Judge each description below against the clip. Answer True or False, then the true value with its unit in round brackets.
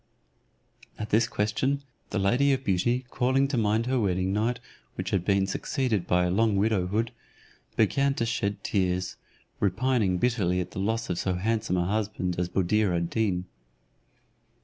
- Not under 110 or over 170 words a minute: True (160 wpm)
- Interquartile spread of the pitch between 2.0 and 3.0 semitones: False (4.1 semitones)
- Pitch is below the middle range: True (105 Hz)